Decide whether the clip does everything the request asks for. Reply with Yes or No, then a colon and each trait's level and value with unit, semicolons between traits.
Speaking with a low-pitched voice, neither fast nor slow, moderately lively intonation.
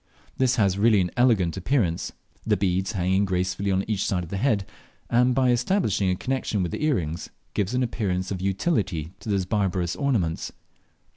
Yes: low, 100 Hz; average, 175 wpm; average, 4.7 semitones